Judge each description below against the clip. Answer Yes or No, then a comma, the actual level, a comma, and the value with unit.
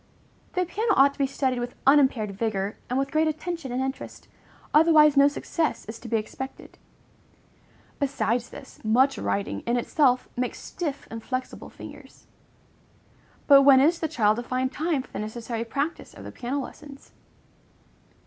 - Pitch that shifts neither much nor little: Yes, average, 3.5 semitones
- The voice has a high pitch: Yes, very high, 265 Hz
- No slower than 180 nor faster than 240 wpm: No, average, 160 wpm